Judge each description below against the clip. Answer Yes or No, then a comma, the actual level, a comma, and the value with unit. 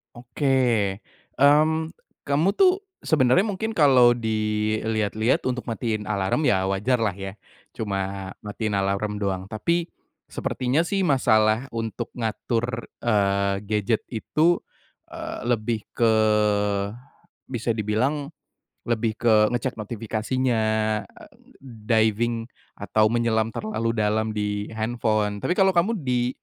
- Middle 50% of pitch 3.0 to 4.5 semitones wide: Yes, average, 3.3 semitones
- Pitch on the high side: No, low, 115 Hz